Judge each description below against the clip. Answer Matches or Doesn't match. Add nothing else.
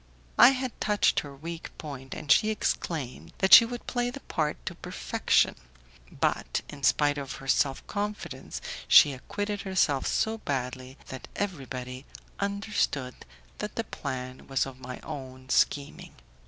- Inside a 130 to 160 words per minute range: Matches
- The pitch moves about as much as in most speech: Doesn't match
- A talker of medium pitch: Matches